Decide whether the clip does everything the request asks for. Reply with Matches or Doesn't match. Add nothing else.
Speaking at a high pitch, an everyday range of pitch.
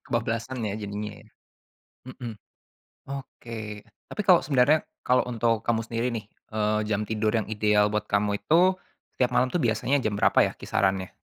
Doesn't match